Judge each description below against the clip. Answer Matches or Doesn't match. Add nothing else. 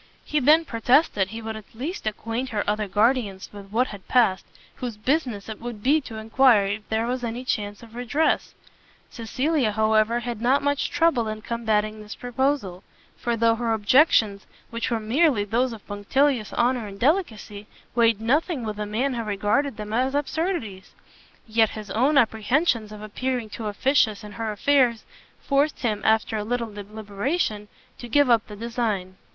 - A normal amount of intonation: Matches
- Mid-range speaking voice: Doesn't match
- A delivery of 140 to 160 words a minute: Doesn't match